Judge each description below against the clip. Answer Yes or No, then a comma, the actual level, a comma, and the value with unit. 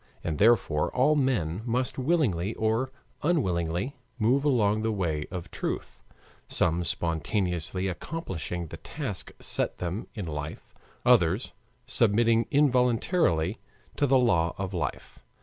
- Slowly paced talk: Yes, slow, 120 wpm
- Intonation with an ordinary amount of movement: No, wide, 6.7 semitones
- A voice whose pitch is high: No, low, 105 Hz